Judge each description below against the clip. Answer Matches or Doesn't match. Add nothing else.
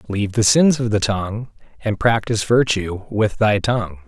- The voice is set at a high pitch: Doesn't match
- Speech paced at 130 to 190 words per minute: Matches